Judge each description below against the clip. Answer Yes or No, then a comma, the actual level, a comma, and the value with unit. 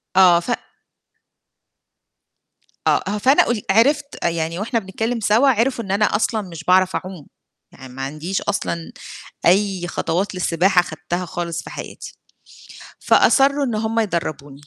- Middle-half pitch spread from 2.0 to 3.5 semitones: No, average, 4.7 semitones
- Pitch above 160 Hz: Yes, high, 190 Hz